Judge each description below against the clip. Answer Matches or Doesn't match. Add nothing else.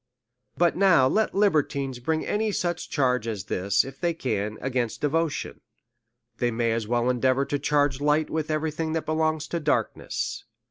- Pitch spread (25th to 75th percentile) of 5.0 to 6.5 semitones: Doesn't match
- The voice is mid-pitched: Matches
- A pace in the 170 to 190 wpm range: Matches